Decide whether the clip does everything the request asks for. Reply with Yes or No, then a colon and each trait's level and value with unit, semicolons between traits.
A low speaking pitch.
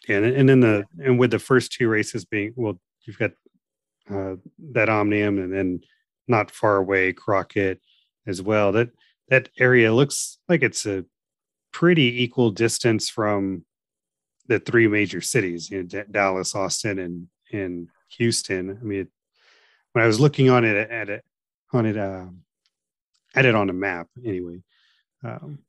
Yes: low, 105 Hz